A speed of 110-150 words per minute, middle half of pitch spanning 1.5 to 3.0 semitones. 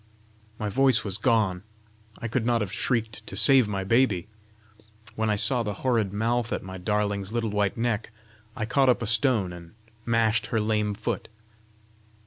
No: average, 170 wpm; narrow, 2.5 semitones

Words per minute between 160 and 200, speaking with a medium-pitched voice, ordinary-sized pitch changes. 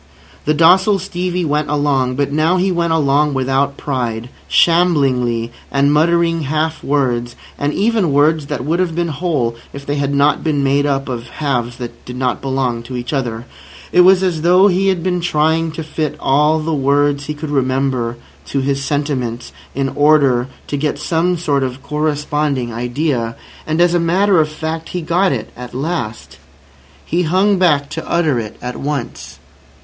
Yes: average, 175 wpm; medium, 145 Hz; average, 3.9 semitones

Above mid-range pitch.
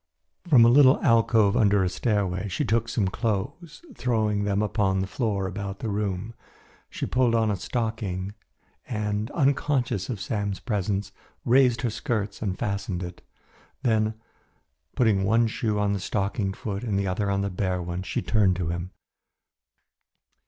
No: low, 105 Hz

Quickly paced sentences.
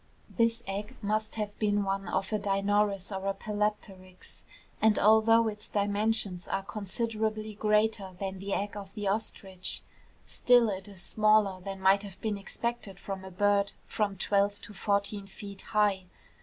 No: average, 155 wpm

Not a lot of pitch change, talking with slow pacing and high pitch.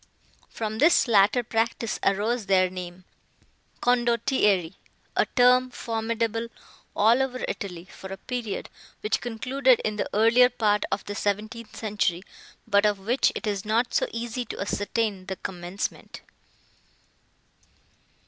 No: average, 3.2 semitones; slow, 125 wpm; high, 220 Hz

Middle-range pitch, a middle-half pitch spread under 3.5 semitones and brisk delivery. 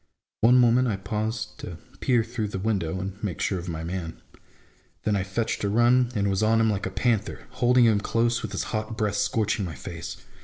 No: low, 105 Hz; average, 3.1 semitones; fast, 215 wpm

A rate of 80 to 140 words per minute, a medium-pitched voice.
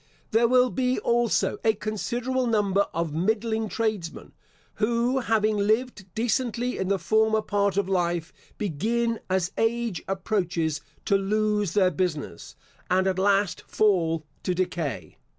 No: slow, 135 wpm; high, 210 Hz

